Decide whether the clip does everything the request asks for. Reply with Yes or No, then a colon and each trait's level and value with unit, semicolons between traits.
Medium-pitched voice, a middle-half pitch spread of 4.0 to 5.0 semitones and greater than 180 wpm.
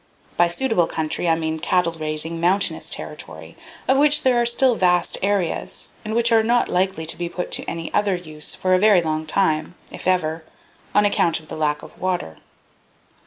Yes: medium, 180 Hz; average, 4.4 semitones; average, 190 wpm